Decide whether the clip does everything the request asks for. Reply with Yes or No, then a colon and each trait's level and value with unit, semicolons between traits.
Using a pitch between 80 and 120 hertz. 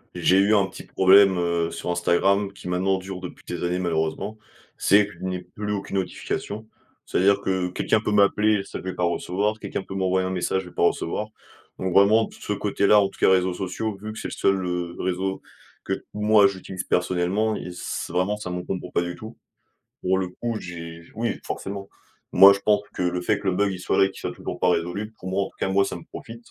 Yes: very low, 95 Hz